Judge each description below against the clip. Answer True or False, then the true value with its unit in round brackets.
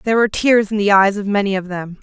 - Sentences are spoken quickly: True (295 wpm)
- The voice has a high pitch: True (205 Hz)